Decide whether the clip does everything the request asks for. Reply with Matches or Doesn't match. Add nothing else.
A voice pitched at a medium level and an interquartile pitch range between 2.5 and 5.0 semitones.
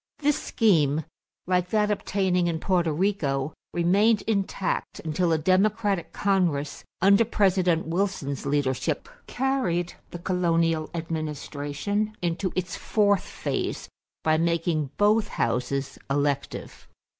Matches